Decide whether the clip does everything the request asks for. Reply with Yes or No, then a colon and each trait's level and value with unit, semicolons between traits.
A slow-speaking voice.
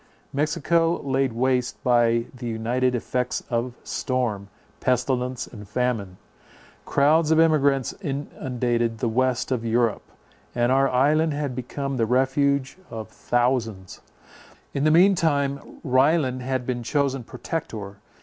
Yes: slow, 125 wpm